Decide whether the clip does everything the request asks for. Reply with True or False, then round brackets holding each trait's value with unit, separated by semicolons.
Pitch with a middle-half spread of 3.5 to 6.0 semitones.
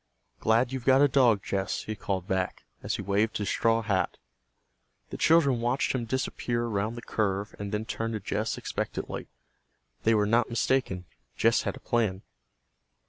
False (3.0 semitones)